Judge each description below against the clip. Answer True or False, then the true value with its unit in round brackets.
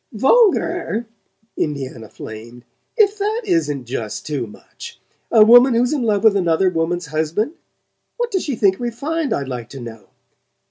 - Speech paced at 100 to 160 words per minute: True (150 wpm)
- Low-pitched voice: False (200 Hz)